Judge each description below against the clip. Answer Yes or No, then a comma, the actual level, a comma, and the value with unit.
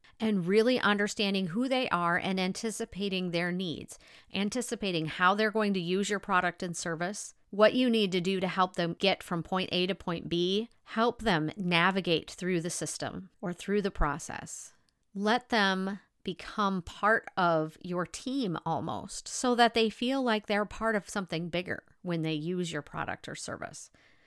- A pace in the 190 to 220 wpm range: No, average, 175 wpm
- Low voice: No, high, 190 Hz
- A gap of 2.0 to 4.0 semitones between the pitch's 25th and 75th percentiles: Yes, average, 3.4 semitones